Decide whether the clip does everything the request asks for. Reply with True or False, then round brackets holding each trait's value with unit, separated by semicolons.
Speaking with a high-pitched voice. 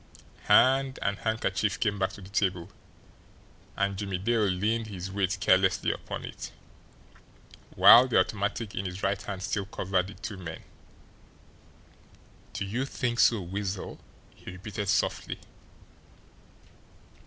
False (100 Hz)